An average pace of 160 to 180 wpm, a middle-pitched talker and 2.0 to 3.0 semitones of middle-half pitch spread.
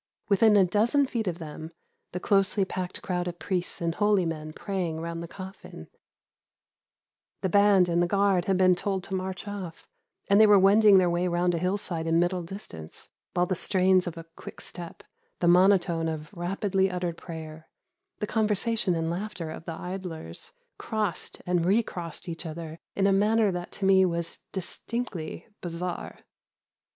Yes: average, 170 wpm; medium, 180 Hz; average, 2.7 semitones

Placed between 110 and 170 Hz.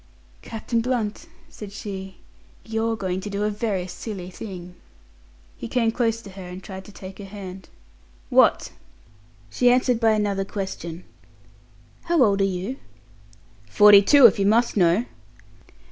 No: high, 205 Hz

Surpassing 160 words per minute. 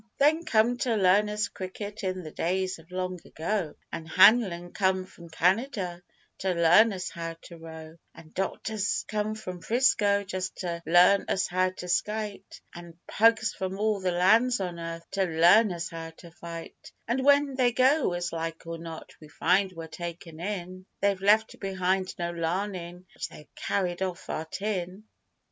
Yes: average, 170 wpm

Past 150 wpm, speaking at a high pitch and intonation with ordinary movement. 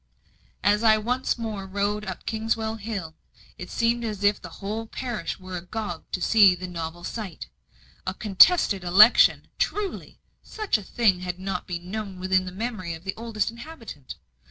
Yes: average, 165 wpm; high, 205 Hz; average, 3.4 semitones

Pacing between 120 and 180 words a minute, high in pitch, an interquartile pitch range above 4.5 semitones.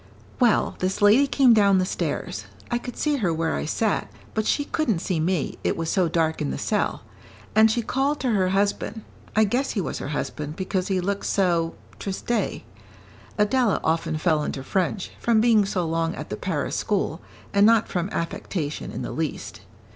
No: average, 190 wpm; high, 195 Hz; average, 5.2 semitones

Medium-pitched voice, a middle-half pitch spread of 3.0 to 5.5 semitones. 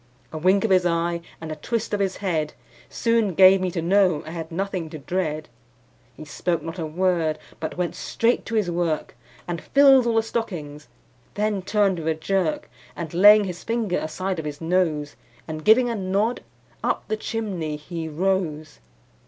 Yes: medium, 180 Hz; average, 4.1 semitones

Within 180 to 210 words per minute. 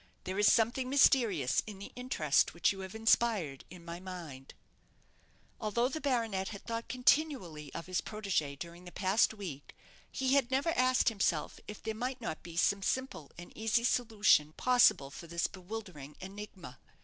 No: average, 165 wpm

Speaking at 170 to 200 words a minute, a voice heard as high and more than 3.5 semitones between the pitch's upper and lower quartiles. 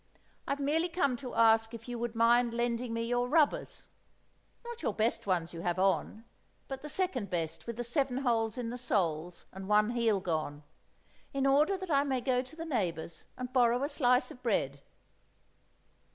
Yes: average, 180 wpm; high, 240 Hz; average, 4.6 semitones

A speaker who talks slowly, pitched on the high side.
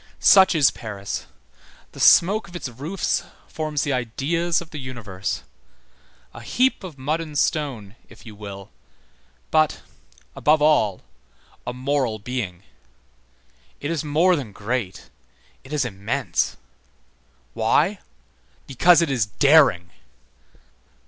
No: slow, 120 wpm; medium, 140 Hz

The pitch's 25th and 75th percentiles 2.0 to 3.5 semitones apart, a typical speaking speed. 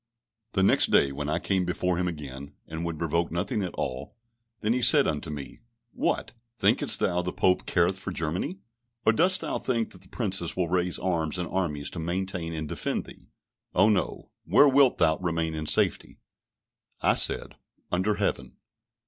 Yes: average, 3.1 semitones; average, 180 wpm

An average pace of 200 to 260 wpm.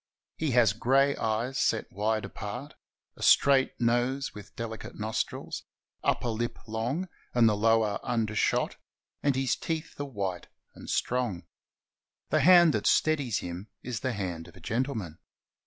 No: average, 145 wpm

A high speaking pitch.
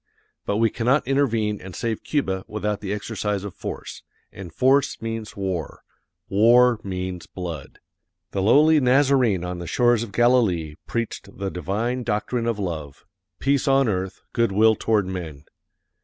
No: low, 105 Hz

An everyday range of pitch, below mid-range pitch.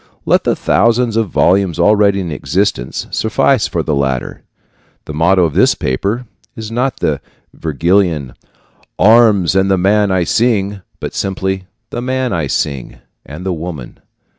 Yes: average, 4.7 semitones; very low, 95 Hz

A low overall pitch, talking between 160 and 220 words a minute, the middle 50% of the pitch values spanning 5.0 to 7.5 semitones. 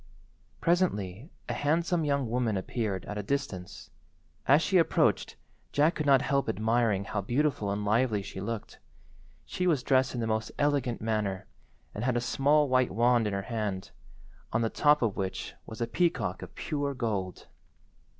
Yes: low, 120 Hz; average, 170 wpm; wide, 5.4 semitones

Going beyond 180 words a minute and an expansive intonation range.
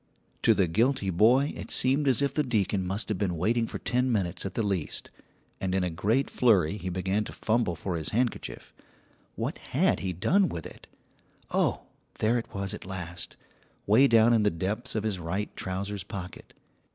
No: average, 190 wpm; average, 4.1 semitones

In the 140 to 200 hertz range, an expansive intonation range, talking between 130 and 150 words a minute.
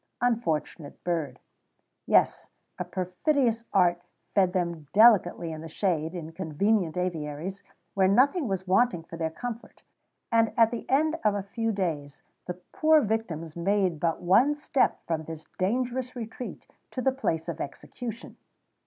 Yes: high, 190 Hz; wide, 5.9 semitones; average, 145 wpm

